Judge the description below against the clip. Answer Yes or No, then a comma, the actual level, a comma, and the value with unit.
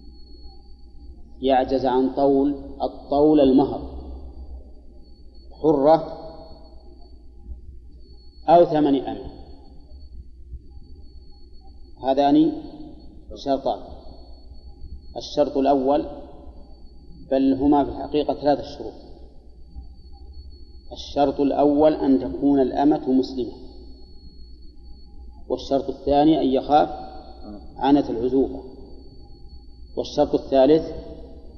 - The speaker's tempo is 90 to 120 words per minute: No, slow, 65 wpm